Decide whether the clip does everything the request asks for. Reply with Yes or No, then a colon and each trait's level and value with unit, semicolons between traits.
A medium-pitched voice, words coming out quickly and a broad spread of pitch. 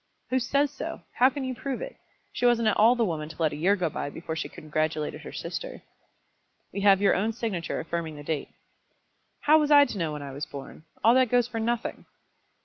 No: high, 205 Hz; fast, 225 wpm; wide, 7.8 semitones